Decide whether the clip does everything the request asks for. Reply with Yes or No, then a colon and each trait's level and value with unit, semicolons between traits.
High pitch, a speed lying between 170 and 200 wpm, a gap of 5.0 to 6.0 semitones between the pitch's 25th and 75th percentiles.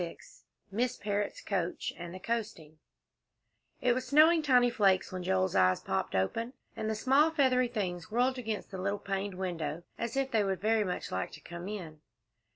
Yes: high, 205 Hz; average, 180 wpm; average, 5.3 semitones